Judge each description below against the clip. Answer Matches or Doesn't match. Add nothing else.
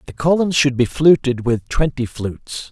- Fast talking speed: Doesn't match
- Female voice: Doesn't match